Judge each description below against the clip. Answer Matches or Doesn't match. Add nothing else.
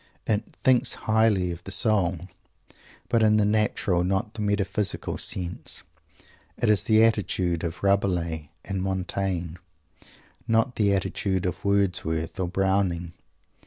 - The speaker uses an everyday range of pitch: Matches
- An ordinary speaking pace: Doesn't match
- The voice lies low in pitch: Matches